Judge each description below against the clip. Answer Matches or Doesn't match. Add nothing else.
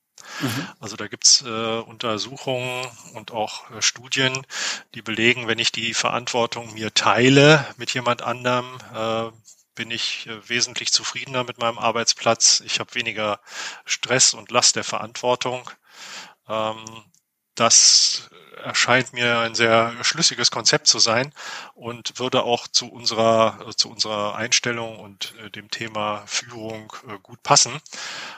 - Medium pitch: Doesn't match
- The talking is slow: Doesn't match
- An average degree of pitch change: Doesn't match